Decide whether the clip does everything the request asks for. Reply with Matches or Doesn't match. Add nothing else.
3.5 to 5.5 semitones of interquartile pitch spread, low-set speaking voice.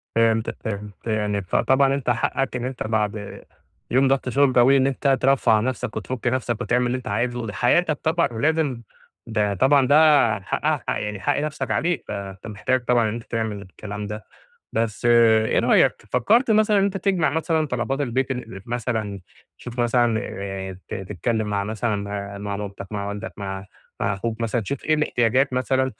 Matches